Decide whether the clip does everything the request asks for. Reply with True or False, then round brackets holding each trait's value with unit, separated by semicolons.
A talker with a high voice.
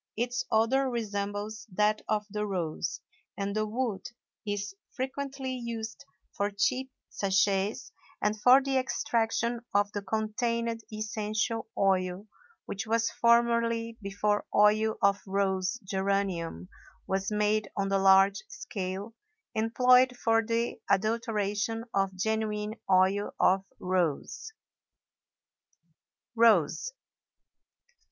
True (210 Hz)